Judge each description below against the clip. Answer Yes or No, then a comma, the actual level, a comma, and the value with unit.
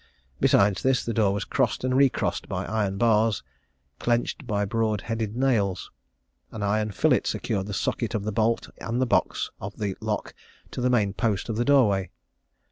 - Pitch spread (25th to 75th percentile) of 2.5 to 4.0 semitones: Yes, average, 2.8 semitones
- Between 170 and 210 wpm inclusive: Yes, average, 185 wpm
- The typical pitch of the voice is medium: No, low, 110 Hz